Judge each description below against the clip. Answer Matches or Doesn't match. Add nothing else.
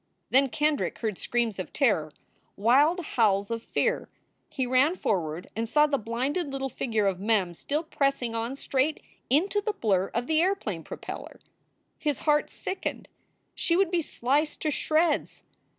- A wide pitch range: Matches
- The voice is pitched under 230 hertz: Doesn't match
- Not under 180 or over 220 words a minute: Doesn't match